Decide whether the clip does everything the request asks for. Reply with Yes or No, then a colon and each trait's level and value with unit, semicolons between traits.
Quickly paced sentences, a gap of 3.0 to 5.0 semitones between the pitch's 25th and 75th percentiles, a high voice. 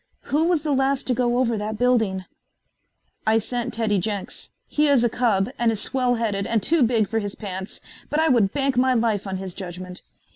Yes: fast, 210 wpm; average, 4.0 semitones; high, 230 Hz